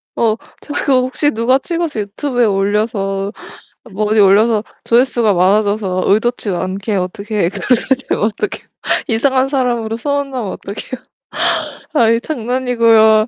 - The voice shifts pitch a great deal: No, average, 3.7 semitones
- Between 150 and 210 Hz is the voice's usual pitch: No, high, 225 Hz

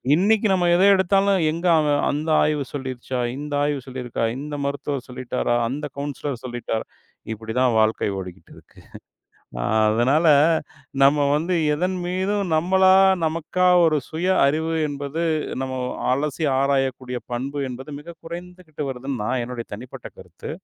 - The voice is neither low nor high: Yes, medium, 145 Hz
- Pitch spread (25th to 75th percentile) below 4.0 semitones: No, average, 4.7 semitones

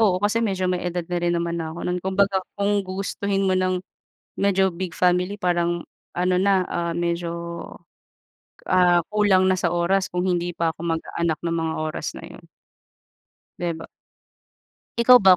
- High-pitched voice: No, medium, 180 Hz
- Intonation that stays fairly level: Yes, narrow, 1.9 semitones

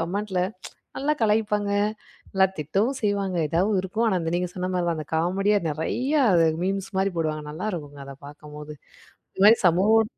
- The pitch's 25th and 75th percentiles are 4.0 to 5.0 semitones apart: Yes, average, 4.4 semitones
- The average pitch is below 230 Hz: Yes, high, 190 Hz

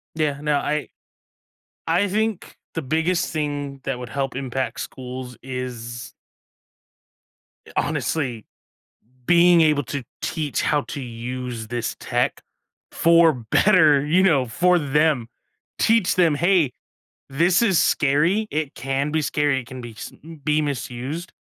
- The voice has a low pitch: No, medium, 145 Hz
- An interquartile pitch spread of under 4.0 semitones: No, average, 4.3 semitones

